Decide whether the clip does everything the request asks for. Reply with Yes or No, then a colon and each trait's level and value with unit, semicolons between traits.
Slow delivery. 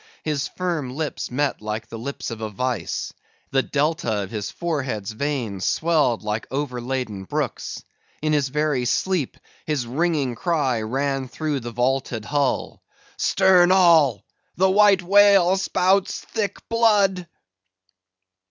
Yes: slow, 130 wpm